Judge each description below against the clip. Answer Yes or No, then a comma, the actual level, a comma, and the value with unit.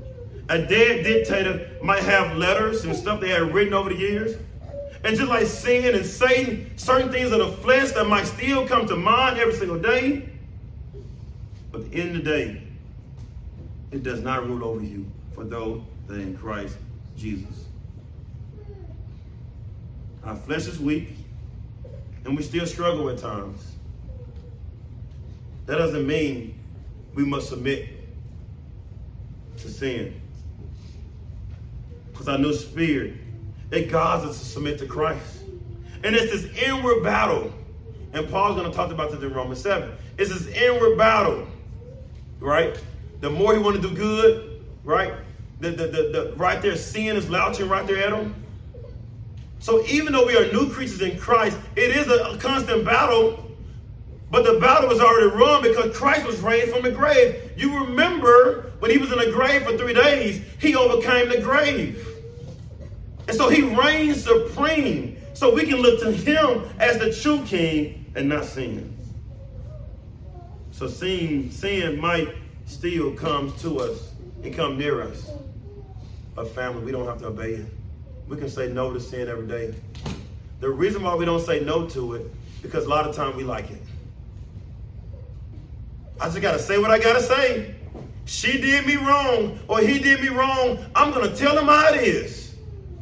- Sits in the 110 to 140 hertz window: No, medium, 150 Hz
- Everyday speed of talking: Yes, average, 165 wpm